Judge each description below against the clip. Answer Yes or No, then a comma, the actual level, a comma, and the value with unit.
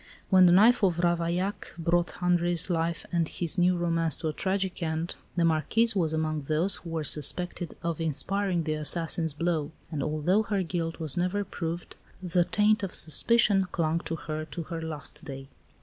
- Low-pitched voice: No, medium, 170 Hz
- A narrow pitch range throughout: Yes, narrow, 2.3 semitones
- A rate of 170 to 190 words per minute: Yes, average, 180 wpm